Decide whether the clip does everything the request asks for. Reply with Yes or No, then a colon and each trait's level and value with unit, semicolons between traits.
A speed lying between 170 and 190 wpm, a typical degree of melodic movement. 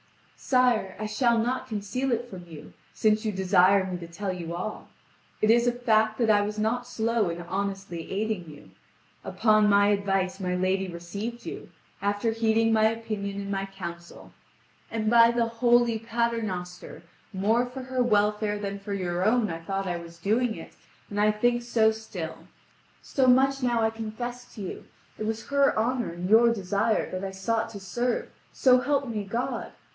Yes: average, 180 wpm; average, 3.4 semitones